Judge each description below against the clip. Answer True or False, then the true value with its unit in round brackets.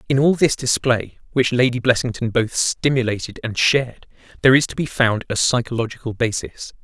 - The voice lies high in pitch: False (125 Hz)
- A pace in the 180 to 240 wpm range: False (165 wpm)